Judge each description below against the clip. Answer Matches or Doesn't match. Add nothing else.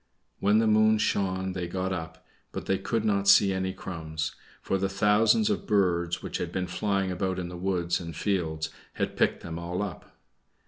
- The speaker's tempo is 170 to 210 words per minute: Matches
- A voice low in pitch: Matches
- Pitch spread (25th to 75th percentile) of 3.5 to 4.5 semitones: Doesn't match